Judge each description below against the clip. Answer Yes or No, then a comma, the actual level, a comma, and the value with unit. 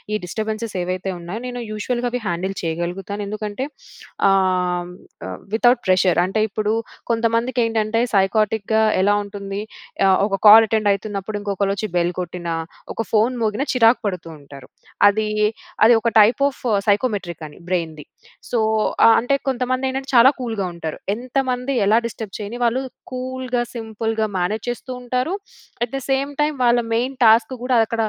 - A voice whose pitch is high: Yes, high, 220 Hz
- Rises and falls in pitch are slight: No, average, 3.8 semitones